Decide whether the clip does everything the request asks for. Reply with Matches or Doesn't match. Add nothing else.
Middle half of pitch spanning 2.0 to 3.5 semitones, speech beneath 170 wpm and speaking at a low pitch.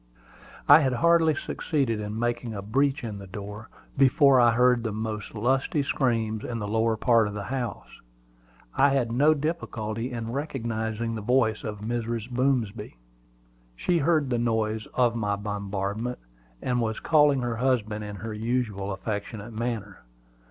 Matches